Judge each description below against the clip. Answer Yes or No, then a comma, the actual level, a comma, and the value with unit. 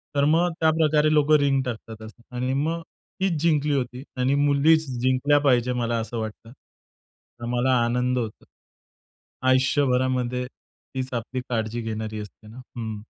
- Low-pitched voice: Yes, low, 130 Hz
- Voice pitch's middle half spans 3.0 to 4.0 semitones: Yes, average, 3.4 semitones